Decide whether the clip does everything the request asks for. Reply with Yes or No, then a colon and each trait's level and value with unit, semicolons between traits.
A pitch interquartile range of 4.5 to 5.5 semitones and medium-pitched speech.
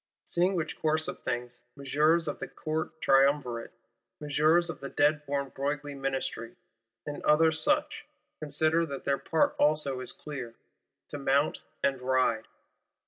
No: narrow, 2.5 semitones; medium, 145 Hz